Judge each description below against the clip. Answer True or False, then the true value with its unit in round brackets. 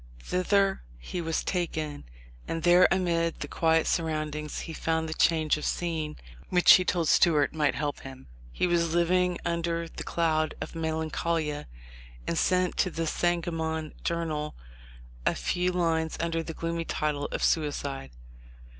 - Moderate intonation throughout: False (1.8 semitones)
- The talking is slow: False (150 wpm)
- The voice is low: False (165 Hz)